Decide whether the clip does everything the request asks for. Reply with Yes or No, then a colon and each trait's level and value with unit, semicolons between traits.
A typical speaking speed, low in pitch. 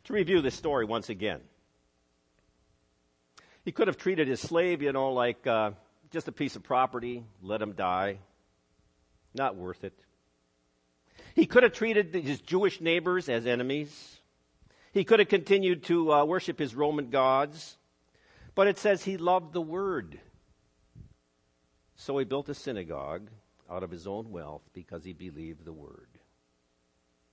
Yes: average, 150 wpm; low, 110 Hz